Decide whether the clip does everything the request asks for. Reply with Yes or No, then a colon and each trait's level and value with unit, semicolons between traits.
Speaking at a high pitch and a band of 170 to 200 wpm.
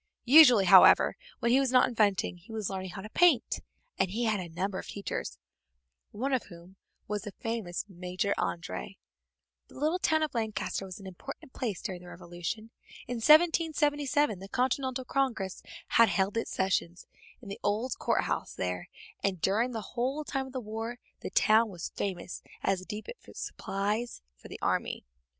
Yes: high, 215 Hz; average, 175 wpm